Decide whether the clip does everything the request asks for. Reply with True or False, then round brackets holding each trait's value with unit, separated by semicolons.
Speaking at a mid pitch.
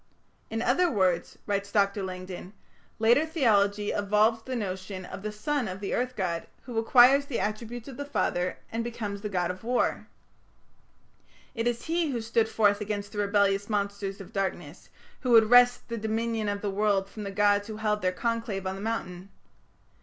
False (210 Hz)